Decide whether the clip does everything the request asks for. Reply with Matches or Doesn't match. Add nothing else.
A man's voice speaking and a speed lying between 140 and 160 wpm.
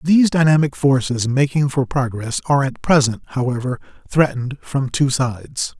Matches